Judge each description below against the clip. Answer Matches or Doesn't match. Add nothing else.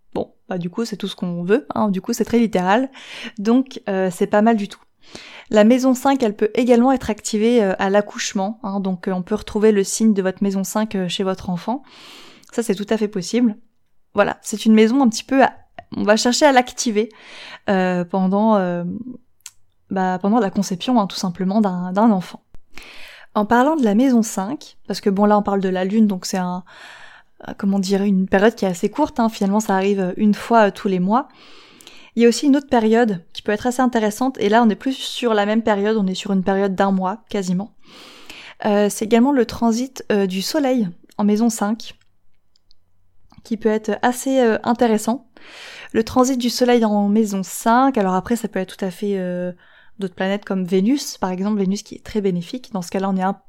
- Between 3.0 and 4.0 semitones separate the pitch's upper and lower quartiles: Matches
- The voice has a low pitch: Doesn't match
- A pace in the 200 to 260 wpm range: Matches